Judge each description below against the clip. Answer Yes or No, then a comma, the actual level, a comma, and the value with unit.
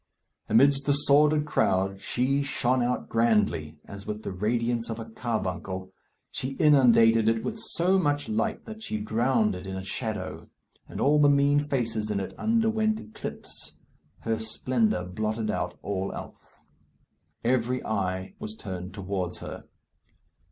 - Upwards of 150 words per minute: No, average, 145 wpm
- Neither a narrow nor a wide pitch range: No, wide, 5.8 semitones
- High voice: No, low, 115 Hz